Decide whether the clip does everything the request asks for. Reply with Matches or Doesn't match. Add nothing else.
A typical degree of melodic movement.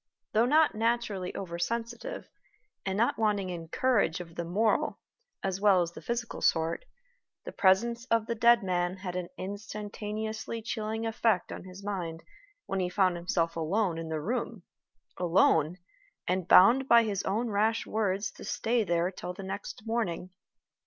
Matches